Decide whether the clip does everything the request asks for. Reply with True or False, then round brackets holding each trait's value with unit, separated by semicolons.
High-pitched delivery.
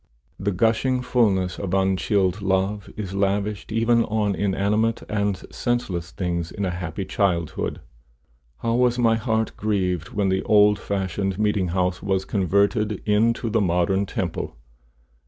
False (100 Hz)